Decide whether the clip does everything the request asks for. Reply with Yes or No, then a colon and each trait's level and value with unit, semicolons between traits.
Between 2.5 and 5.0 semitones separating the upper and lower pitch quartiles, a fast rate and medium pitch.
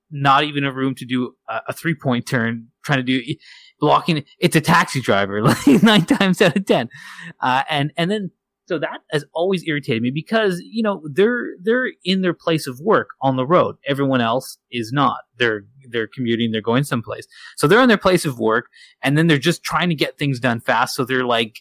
No: wide, 5.6 semitones; fast, 210 wpm; medium, 145 Hz